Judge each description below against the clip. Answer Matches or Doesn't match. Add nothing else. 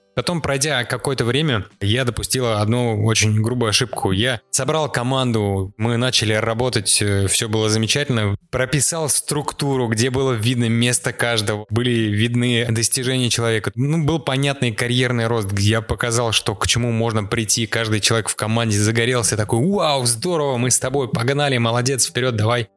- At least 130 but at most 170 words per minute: Matches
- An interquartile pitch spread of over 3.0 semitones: Doesn't match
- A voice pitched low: Matches